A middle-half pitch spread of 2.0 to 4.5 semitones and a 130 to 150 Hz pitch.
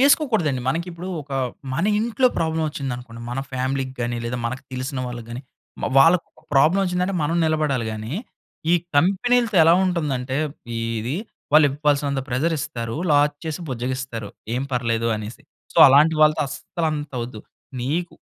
No: average, 5.0 semitones; medium, 140 Hz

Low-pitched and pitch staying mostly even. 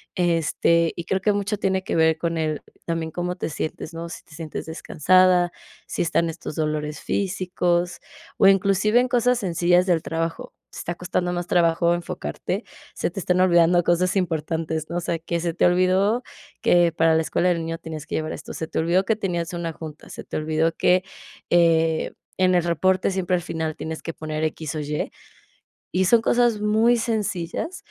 No: medium, 175 Hz; narrow, 2.3 semitones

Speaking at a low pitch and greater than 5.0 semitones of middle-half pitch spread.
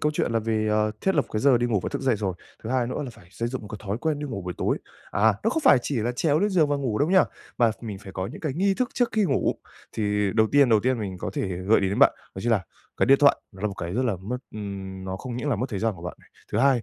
Yes: low, 115 Hz; wide, 5.6 semitones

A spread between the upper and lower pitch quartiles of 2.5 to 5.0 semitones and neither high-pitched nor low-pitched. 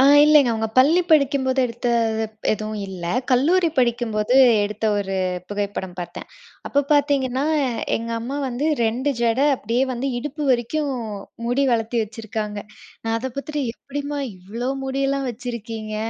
No: average, 3.9 semitones; high, 245 Hz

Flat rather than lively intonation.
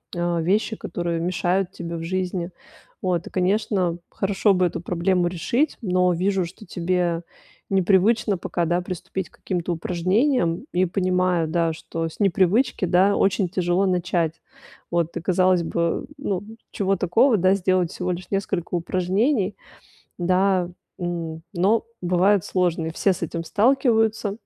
Yes: narrow, 2.2 semitones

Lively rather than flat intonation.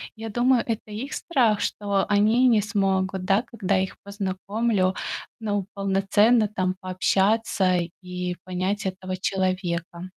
No: narrow, 2.5 semitones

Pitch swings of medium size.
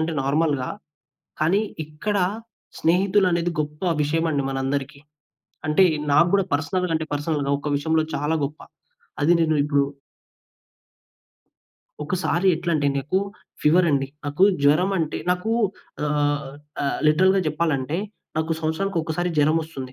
Yes: average, 3.0 semitones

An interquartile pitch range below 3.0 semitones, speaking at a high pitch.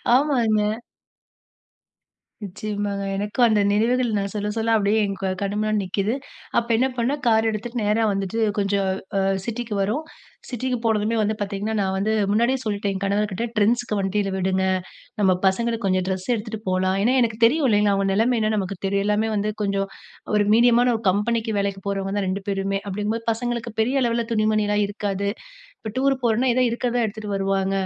Yes: narrow, 2.6 semitones; high, 210 Hz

